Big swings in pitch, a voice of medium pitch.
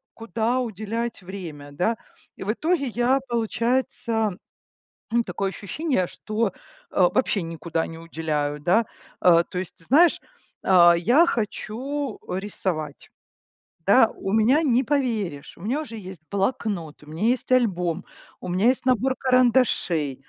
No: wide, 6.0 semitones; high, 215 Hz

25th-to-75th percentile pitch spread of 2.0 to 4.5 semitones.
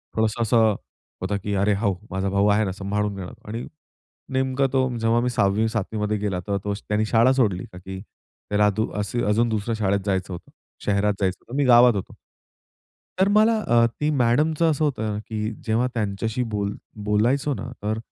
Yes: average, 2.9 semitones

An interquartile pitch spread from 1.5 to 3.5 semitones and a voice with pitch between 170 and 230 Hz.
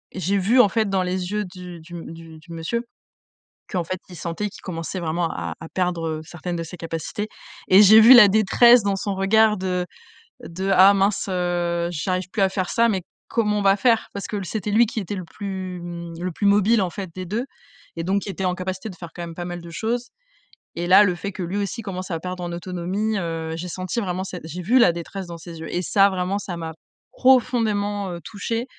Yes: average, 2.9 semitones; medium, 185 Hz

